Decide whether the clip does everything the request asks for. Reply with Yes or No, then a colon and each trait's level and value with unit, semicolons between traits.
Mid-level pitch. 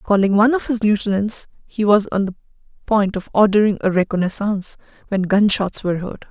No: high, 205 Hz